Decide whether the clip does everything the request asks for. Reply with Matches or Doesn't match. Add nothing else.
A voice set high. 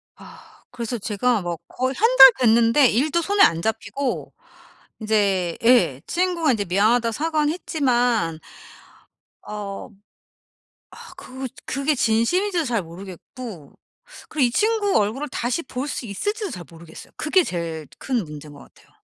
Matches